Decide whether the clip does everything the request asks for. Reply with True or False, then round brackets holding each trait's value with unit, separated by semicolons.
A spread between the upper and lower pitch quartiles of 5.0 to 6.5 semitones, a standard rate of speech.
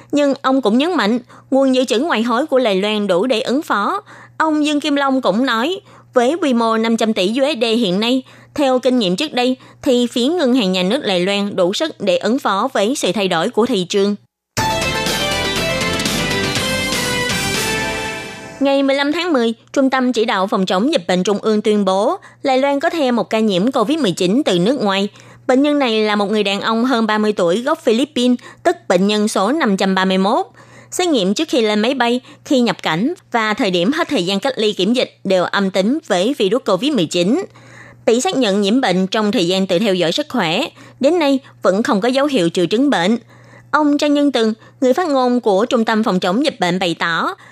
True (5.4 semitones; 210 wpm)